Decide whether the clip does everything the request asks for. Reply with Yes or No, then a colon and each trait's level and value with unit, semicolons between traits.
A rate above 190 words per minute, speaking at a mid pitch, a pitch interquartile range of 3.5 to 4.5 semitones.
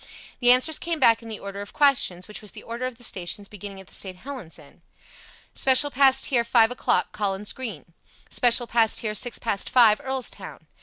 No: average, 200 wpm; high, 230 Hz; average, 4.1 semitones